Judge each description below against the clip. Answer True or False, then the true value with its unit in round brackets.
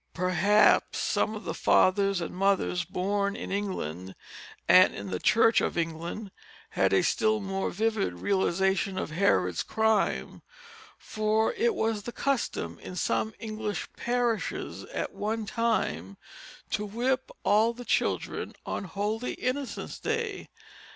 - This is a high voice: True (205 Hz)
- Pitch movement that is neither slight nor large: True (3.7 semitones)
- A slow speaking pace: True (130 wpm)